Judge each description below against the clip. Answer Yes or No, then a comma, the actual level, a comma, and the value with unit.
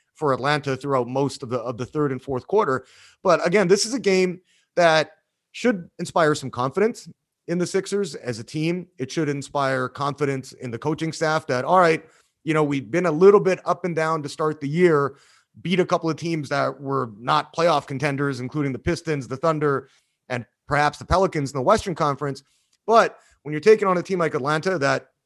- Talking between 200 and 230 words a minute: Yes, fast, 205 wpm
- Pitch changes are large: No, average, 4.2 semitones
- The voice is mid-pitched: Yes, medium, 150 Hz